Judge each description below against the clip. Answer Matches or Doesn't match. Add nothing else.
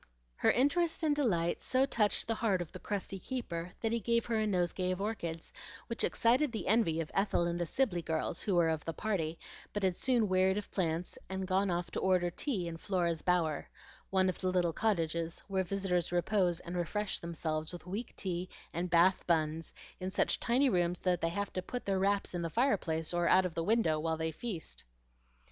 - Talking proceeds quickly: Matches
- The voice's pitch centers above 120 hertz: Matches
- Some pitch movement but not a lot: Matches